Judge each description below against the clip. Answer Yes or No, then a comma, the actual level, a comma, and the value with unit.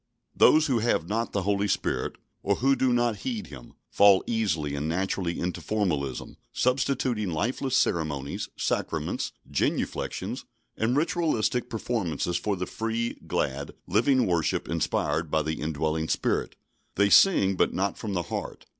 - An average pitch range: No, wide, 6.7 semitones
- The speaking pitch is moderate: No, low, 100 Hz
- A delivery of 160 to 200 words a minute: No, average, 145 wpm